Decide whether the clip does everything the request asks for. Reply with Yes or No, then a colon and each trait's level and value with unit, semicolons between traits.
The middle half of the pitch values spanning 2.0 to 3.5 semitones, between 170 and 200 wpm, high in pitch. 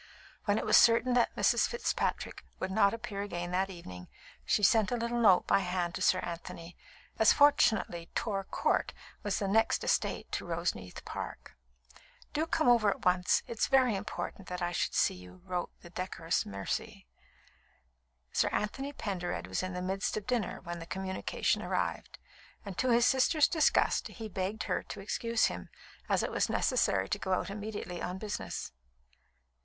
No: average, 4.4 semitones; average, 175 wpm; high, 195 Hz